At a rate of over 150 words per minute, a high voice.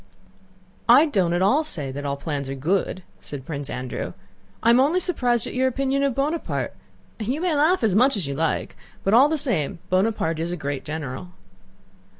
Yes: average, 195 wpm; high, 200 Hz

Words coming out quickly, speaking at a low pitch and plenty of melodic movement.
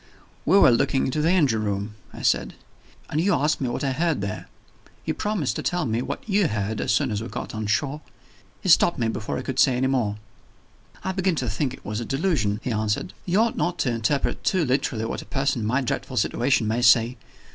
Yes: fast, 230 wpm; low, 130 Hz; wide, 5.7 semitones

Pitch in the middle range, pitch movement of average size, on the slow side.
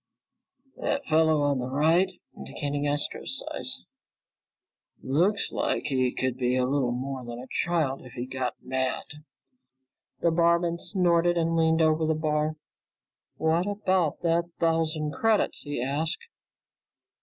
Yes: medium, 155 Hz; average, 4.2 semitones; slow, 130 wpm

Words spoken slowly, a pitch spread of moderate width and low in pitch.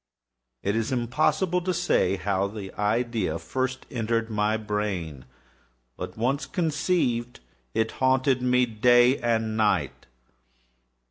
Yes: slow, 115 wpm; average, 3.6 semitones; low, 115 Hz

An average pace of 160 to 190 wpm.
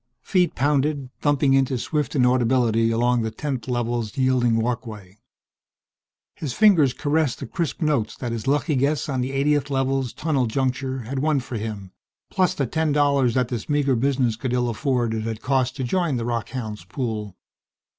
Yes: average, 170 wpm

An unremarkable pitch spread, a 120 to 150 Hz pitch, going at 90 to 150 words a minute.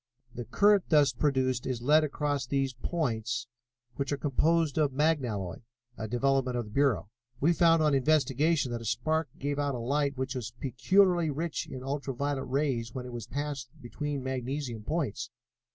No: average, 3.3 semitones; low, 135 Hz; average, 170 wpm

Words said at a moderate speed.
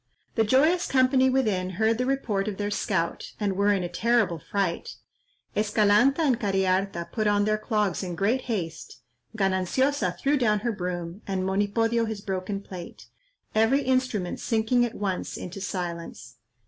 Yes: average, 155 wpm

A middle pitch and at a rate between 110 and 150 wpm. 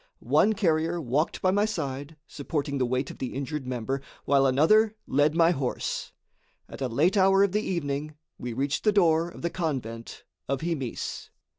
No: medium, 150 Hz; average, 175 wpm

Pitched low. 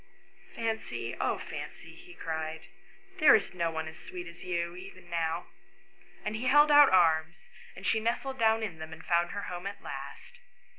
No: medium, 180 Hz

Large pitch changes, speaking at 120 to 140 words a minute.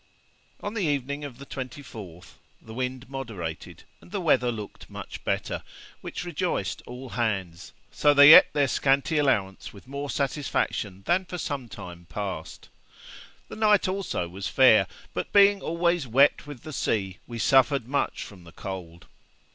No: wide, 7.0 semitones; average, 160 wpm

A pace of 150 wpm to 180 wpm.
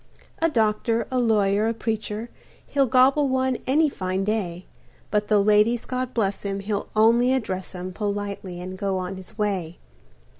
Yes: average, 160 wpm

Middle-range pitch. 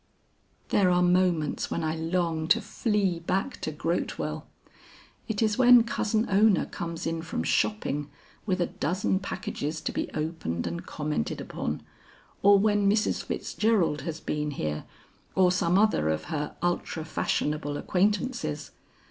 Yes: medium, 175 Hz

